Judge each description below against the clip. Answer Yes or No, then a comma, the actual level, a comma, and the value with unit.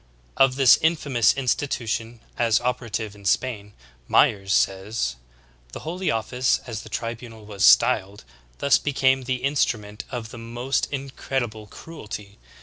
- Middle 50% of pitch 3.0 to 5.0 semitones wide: Yes, average, 3.8 semitones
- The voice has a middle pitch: No, low, 115 Hz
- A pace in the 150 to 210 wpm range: No, average, 140 wpm